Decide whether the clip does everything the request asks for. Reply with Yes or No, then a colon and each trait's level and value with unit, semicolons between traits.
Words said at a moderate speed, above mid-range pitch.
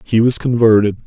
No: average, 170 wpm; low, 115 Hz